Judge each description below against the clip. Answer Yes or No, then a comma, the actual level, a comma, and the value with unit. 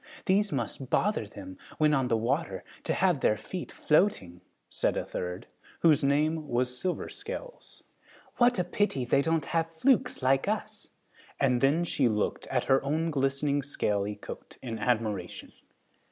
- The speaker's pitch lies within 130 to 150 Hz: Yes, medium, 140 Hz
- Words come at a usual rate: Yes, average, 155 wpm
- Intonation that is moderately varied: No, wide, 5.7 semitones